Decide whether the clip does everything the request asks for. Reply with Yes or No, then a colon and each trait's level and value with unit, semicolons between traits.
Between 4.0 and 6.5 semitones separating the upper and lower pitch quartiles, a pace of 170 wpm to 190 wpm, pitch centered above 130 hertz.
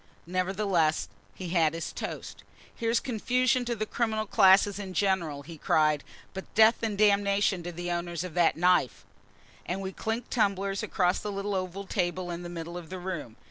No: average, 3.0 semitones; average, 180 wpm; high, 190 Hz